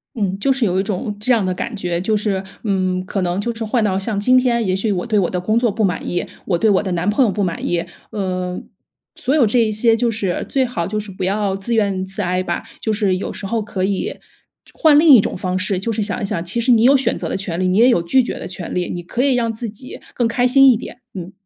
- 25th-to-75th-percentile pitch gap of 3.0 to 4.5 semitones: Yes, average, 3.9 semitones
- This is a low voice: No, high, 205 Hz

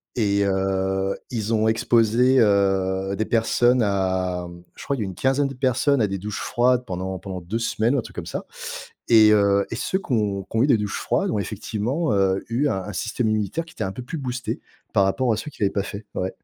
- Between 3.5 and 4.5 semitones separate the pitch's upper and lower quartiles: Yes, average, 4.0 semitones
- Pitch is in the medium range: No, low, 105 Hz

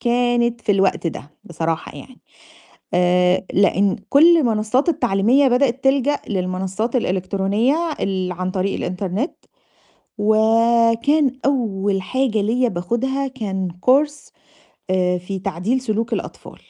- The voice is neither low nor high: No, high, 220 Hz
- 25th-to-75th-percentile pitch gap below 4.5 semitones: No, average, 5.1 semitones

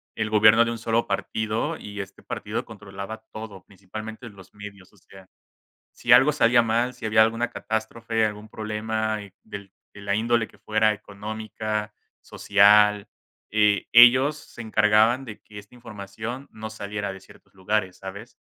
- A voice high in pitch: No, low, 110 Hz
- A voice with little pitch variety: Yes, narrow, 1.7 semitones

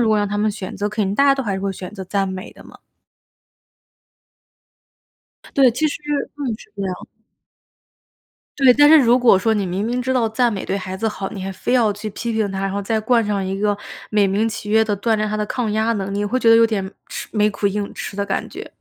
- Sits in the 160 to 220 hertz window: Yes, high, 210 Hz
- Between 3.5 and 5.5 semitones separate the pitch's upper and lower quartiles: No, narrow, 2.6 semitones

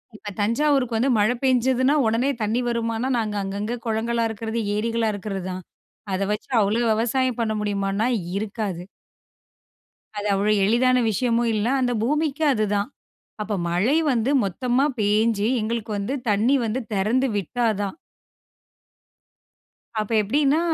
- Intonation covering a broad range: No, average, 3.1 semitones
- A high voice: Yes, high, 225 Hz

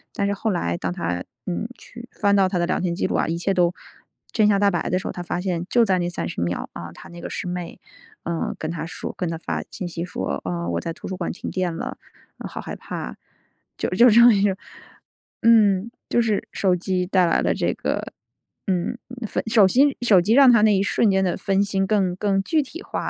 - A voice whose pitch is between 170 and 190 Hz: Yes, medium, 185 Hz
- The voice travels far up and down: No, average, 3.3 semitones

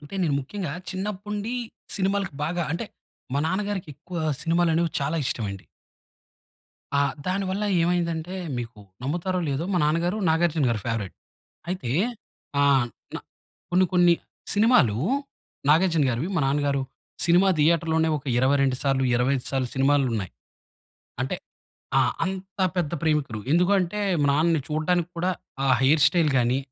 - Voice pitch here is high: No, medium, 165 Hz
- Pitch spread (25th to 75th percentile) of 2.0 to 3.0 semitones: No, average, 4.8 semitones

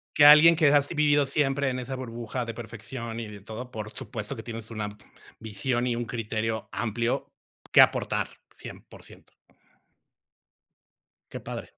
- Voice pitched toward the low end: Yes, low, 120 Hz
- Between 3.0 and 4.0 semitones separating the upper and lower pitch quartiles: Yes, average, 3.4 semitones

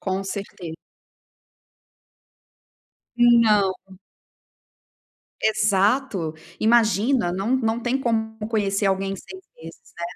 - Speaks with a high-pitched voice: Yes, high, 215 Hz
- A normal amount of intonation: Yes, average, 3.5 semitones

